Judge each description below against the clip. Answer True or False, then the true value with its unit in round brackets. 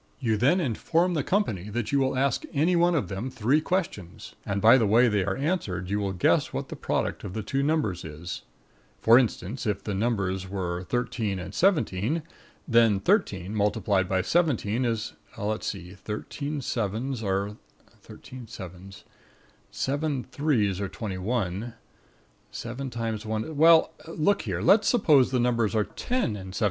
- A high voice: False (115 Hz)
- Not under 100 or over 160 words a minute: False (170 wpm)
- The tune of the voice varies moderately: False (6.1 semitones)